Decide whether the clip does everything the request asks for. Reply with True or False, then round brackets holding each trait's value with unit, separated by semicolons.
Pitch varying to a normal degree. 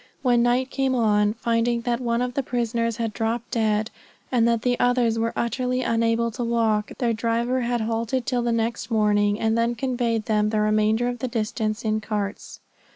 False (1.7 semitones)